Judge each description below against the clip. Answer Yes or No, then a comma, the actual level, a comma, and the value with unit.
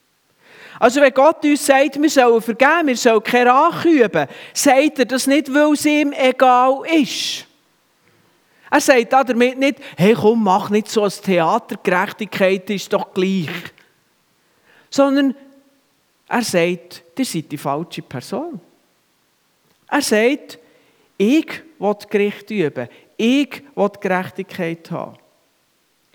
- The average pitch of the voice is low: No, high, 235 Hz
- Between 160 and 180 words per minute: No, average, 130 wpm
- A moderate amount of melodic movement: No, wide, 6.2 semitones